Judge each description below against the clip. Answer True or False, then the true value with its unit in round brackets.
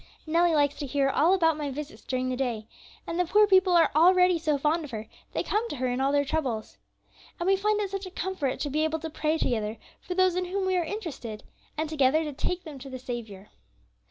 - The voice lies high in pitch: True (310 Hz)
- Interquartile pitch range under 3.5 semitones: False (5.2 semitones)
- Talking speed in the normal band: False (245 wpm)